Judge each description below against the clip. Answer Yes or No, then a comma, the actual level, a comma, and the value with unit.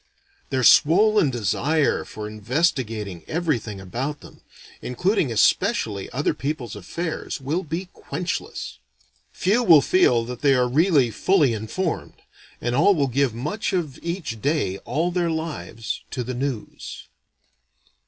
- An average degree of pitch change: No, wide, 6.3 semitones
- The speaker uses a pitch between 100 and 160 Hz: Yes, medium, 140 Hz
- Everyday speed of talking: No, slow, 130 wpm